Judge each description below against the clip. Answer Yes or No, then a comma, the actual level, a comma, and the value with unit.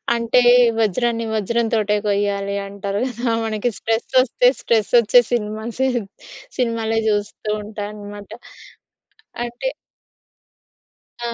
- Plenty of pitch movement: No, narrow, 2.4 semitones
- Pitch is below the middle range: No, high, 220 Hz